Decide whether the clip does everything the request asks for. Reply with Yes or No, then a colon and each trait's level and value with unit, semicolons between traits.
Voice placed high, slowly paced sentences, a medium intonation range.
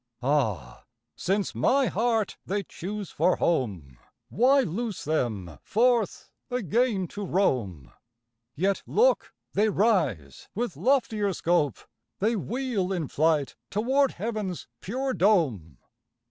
No: high, 195 Hz; slow, 110 wpm; wide, 7.7 semitones